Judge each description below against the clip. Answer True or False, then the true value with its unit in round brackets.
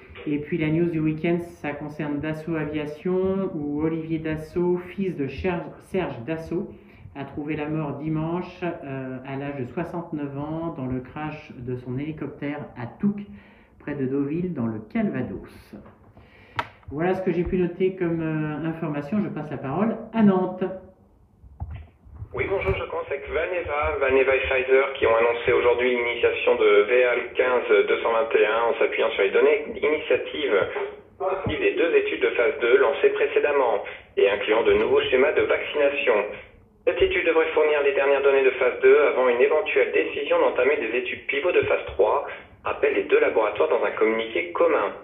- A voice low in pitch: False (180 Hz)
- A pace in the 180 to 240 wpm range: False (165 wpm)